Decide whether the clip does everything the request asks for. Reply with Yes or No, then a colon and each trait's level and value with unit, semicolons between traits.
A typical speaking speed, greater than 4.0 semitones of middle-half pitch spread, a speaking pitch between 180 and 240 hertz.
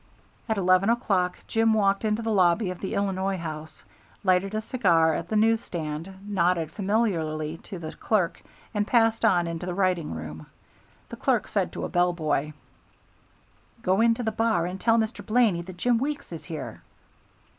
Yes: average, 175 wpm; average, 4.4 semitones; high, 190 Hz